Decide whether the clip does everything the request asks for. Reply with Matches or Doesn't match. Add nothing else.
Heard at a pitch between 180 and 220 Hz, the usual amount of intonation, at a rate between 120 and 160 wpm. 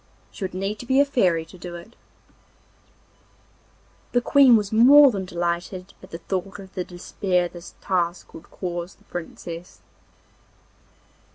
Matches